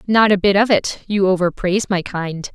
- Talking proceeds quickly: Yes, fast, 210 wpm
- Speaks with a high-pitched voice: Yes, high, 195 Hz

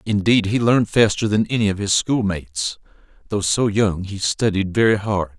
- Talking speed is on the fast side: No, average, 180 wpm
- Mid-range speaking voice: No, low, 100 Hz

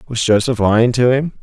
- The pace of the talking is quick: Yes, fast, 210 wpm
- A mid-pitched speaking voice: No, low, 120 Hz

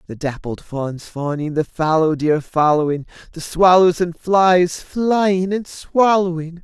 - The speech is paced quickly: No, slow, 135 wpm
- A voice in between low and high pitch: Yes, medium, 170 Hz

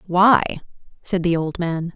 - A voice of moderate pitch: Yes, medium, 180 Hz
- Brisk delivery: No, average, 155 wpm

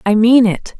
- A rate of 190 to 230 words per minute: Yes, fast, 225 wpm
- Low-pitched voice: No, high, 225 Hz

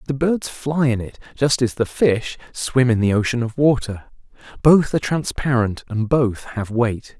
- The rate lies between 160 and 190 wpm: Yes, average, 185 wpm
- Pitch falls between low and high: No, low, 125 Hz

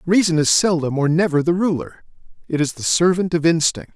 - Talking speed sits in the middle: Yes, average, 195 wpm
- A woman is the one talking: No, male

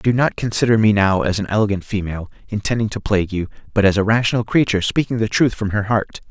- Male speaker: Yes, male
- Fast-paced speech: Yes, fast, 230 wpm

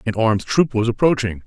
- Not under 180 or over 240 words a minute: Yes, fast, 205 wpm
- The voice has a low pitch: Yes, low, 115 Hz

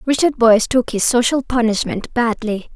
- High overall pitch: Yes, high, 235 Hz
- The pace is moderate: Yes, average, 155 wpm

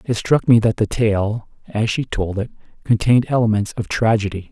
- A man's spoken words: Yes, male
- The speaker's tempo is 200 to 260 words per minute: No, average, 185 wpm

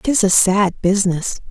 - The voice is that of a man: No, female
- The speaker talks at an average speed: Yes, average, 160 wpm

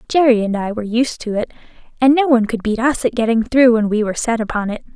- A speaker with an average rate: No, fast, 265 wpm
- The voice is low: No, high, 230 Hz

